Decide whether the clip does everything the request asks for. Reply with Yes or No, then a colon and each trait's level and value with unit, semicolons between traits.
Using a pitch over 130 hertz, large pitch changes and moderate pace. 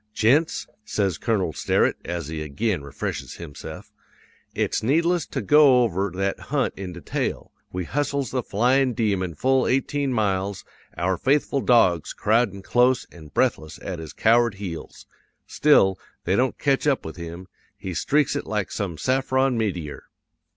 No: low, 105 Hz; wide, 6.7 semitones; average, 150 wpm